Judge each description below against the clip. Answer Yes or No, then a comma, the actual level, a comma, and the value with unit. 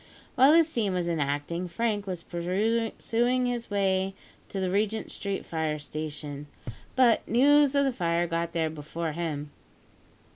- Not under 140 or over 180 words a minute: Yes, average, 145 wpm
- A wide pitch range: Yes, wide, 5.9 semitones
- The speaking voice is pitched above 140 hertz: Yes, medium, 185 Hz